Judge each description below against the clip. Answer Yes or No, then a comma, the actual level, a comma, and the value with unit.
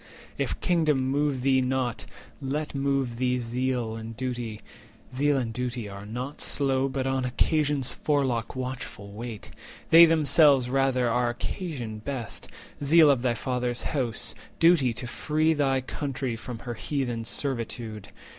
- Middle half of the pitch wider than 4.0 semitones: No, average, 2.8 semitones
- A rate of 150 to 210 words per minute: No, average, 140 wpm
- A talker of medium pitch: No, low, 130 Hz